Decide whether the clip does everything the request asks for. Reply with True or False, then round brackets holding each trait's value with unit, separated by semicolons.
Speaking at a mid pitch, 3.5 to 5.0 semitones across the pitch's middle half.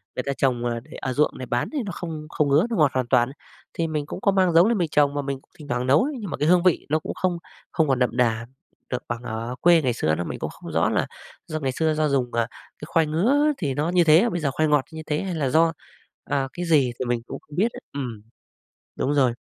True (150 Hz; 4.7 semitones)